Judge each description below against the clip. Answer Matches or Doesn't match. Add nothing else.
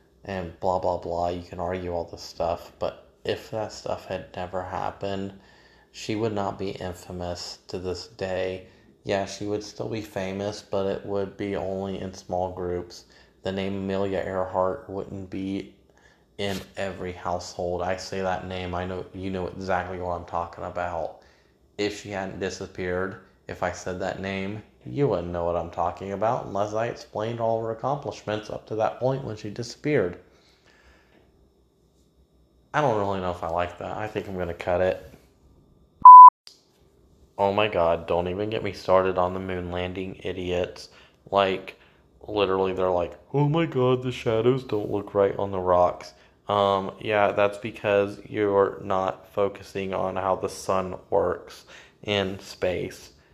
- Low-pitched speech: Matches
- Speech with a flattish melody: Matches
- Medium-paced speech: Matches